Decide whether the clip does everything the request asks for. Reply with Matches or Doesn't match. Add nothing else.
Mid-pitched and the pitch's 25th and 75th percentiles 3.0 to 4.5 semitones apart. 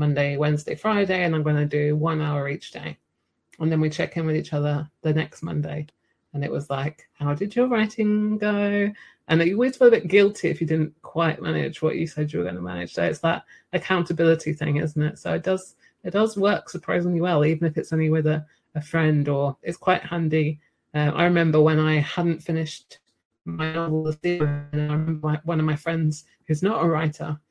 Doesn't match